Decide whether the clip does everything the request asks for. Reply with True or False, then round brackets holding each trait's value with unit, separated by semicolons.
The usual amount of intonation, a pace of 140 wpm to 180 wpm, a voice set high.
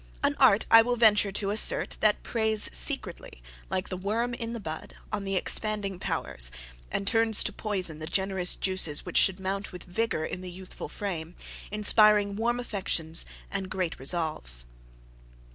True (3.2 semitones; 160 wpm; 195 Hz)